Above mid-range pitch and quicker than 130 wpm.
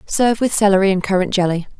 Yes: high, 195 Hz; average, 200 wpm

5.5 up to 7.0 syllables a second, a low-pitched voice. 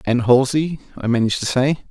Yes: 5.9 syllables/s; low, 130 Hz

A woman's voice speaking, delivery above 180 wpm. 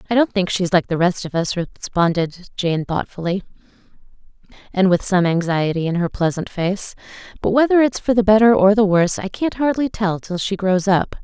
Yes: female; average, 200 wpm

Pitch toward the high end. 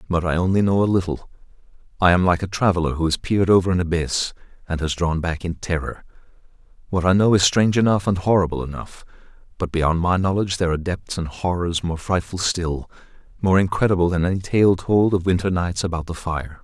No: very low, 90 Hz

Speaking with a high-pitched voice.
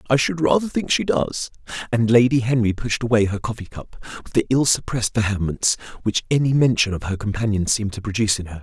No: low, 115 Hz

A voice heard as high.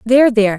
Yes: high, 230 Hz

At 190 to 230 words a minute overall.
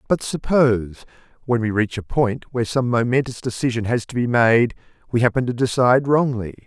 No: average, 180 wpm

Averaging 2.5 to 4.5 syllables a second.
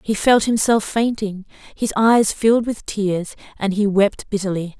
Yes: 4.4 syllables/s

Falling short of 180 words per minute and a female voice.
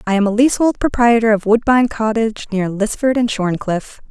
Yes: average, 160 wpm; female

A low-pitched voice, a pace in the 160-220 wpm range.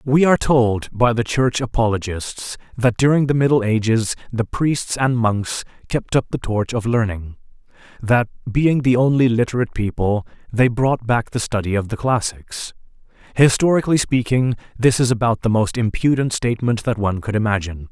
Yes: low, 115 Hz; average, 165 wpm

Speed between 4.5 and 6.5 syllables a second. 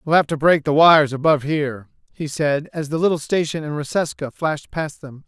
Yes: 5.7 syllables/s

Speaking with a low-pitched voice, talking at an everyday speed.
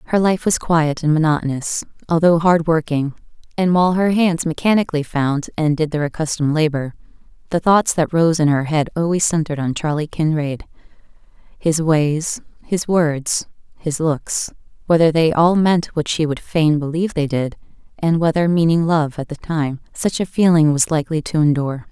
No: medium, 160 Hz; average, 170 wpm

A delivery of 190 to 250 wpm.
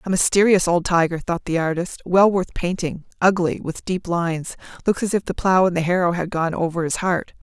Yes: average, 200 wpm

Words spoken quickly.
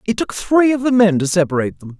Yes: fast, 270 wpm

